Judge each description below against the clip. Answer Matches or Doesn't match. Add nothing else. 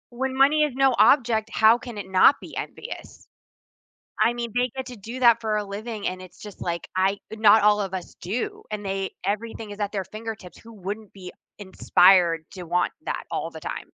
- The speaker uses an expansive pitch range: Doesn't match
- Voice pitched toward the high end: Matches